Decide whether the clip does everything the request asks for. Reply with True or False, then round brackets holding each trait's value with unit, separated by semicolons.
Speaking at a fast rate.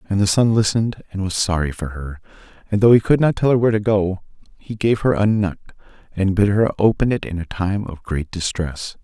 True (230 wpm)